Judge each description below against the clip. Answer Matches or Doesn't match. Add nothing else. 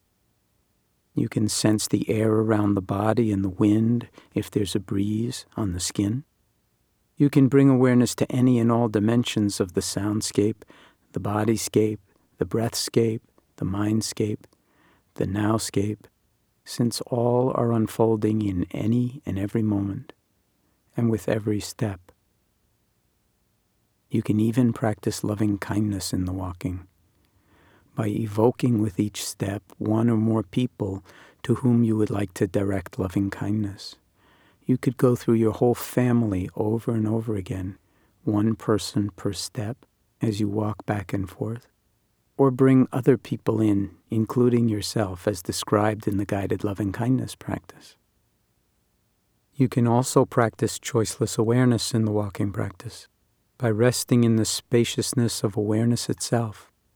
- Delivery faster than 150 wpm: Doesn't match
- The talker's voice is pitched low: Matches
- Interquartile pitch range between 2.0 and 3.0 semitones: Matches